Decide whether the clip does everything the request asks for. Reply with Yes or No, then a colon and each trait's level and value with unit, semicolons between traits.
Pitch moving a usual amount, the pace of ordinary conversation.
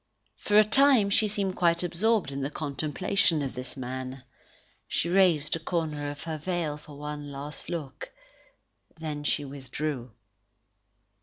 Yes: average, 3.9 semitones; average, 145 wpm